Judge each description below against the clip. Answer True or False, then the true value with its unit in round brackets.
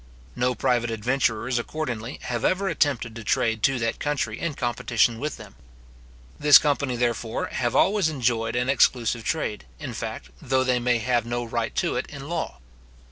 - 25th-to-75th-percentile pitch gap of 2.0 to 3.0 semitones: False (3.4 semitones)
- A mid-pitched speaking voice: False (120 Hz)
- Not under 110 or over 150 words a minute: False (170 wpm)